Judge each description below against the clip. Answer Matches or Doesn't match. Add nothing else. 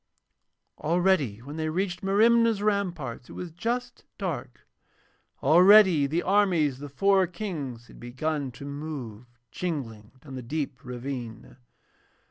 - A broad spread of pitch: Matches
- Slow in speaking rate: Matches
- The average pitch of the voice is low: Doesn't match